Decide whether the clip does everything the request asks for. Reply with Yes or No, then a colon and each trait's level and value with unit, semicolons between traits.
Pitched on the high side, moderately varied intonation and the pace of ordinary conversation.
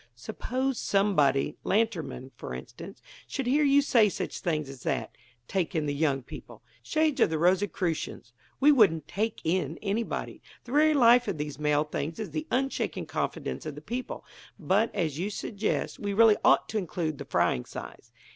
No: high, 195 Hz; wide, 7.4 semitones; average, 175 wpm